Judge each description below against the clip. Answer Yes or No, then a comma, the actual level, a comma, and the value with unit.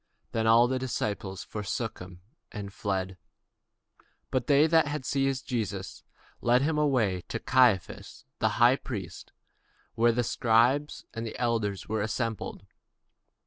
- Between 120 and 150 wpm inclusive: Yes, average, 145 wpm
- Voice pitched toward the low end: Yes, low, 115 Hz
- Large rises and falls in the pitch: No, average, 4.2 semitones